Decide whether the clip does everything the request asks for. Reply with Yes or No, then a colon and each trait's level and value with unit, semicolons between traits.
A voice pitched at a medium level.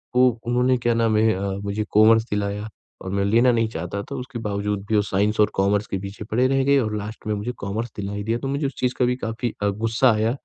No: low, 110 Hz